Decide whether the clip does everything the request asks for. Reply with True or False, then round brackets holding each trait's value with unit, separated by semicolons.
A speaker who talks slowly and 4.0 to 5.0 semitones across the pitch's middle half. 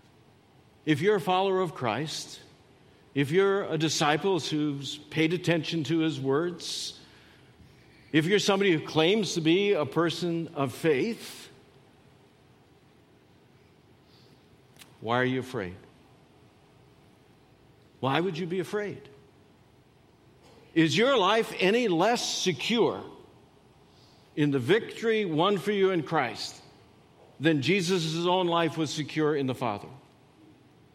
True (115 wpm; 4.6 semitones)